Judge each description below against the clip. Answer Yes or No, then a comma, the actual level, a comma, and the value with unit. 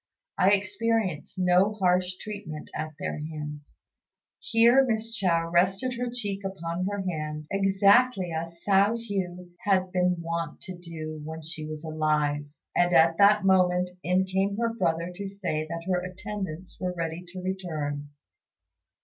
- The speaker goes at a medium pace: Yes, average, 150 wpm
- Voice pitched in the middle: Yes, medium, 180 Hz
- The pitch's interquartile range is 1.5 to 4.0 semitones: Yes, average, 3.3 semitones